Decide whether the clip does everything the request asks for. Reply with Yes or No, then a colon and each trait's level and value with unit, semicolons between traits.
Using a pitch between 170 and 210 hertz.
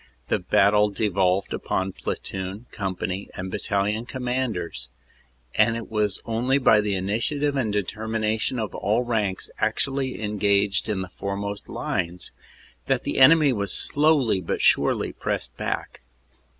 No: low, 105 Hz